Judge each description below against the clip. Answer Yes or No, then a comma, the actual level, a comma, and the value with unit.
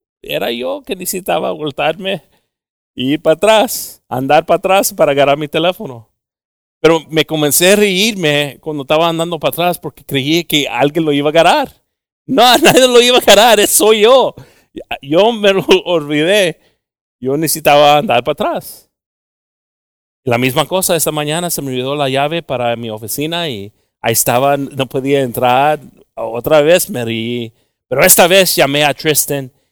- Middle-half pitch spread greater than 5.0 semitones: No, average, 4.5 semitones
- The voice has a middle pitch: Yes, medium, 150 Hz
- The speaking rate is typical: Yes, average, 165 wpm